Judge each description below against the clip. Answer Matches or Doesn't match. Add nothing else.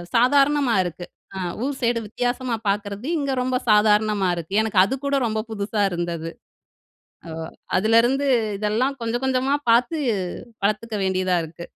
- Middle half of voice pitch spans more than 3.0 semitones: Matches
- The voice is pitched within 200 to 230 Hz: Matches